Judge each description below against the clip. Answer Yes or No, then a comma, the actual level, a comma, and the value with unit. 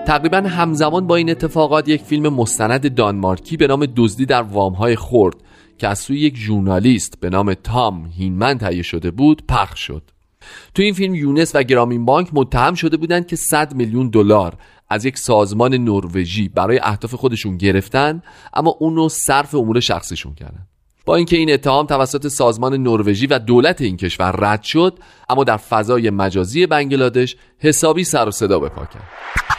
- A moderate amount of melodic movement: No, wide, 6.8 semitones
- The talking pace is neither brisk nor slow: No, fast, 170 wpm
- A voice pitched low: Yes, low, 125 Hz